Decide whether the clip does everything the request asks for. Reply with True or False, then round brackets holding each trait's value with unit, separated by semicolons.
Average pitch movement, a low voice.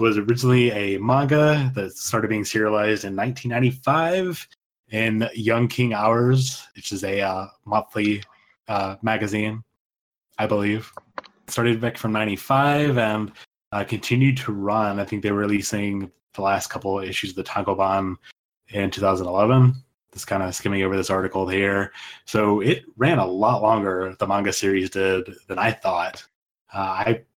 True (3.3 semitones; 105 Hz)